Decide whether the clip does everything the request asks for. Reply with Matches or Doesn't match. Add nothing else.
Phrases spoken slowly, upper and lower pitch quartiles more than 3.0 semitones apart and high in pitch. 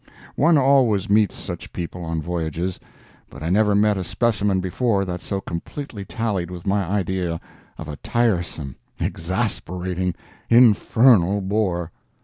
Doesn't match